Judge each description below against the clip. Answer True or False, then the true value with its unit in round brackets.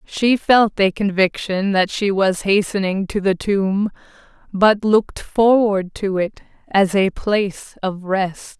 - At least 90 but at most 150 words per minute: True (145 wpm)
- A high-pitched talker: True (200 Hz)